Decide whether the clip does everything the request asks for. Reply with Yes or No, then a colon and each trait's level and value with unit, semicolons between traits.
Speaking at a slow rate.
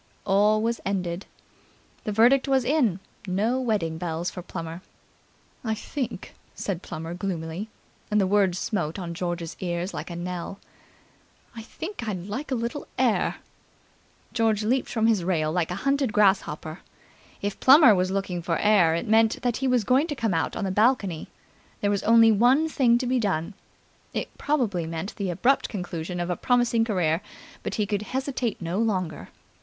No: average, 170 wpm